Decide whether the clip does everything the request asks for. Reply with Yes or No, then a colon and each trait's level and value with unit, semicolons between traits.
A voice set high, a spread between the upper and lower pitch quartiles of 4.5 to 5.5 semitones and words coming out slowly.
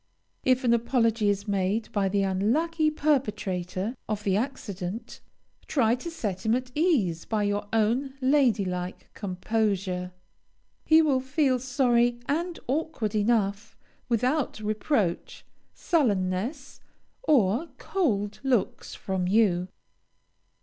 Yes: high, 225 Hz; average, 5.1 semitones; slow, 115 wpm